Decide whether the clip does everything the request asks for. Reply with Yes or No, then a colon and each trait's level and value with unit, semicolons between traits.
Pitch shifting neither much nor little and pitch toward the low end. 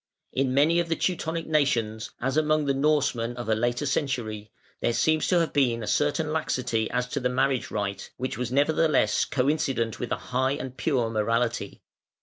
Yes: average, 4.5 semitones; low, 130 Hz